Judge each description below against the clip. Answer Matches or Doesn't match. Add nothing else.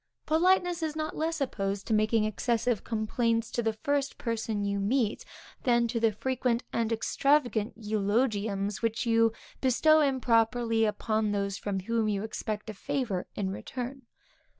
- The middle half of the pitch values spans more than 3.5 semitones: Doesn't match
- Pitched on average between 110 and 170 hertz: Doesn't match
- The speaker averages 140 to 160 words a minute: Matches